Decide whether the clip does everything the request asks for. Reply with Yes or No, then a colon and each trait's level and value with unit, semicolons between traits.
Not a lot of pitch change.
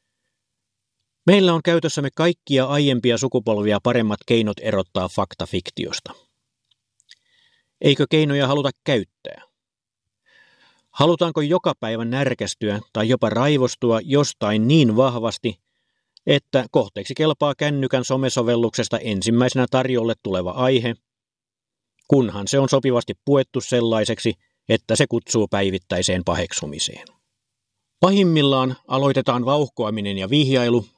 No: average, 4.1 semitones